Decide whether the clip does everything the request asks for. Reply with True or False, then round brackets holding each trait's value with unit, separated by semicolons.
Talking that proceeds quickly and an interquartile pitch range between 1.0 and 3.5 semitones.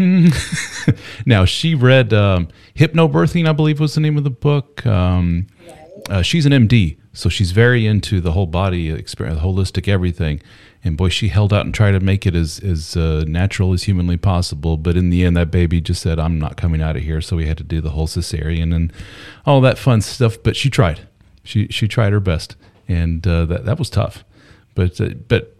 False (210 wpm; 5.2 semitones)